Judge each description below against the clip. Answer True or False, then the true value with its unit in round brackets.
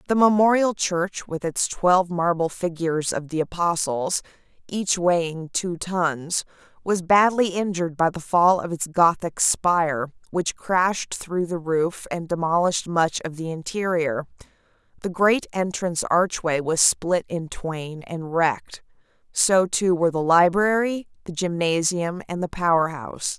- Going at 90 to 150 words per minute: True (145 wpm)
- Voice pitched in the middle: True (175 Hz)